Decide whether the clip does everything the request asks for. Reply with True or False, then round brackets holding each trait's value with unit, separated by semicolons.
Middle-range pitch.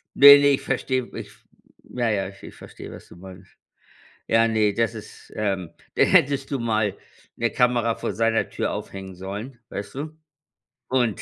False (115 Hz)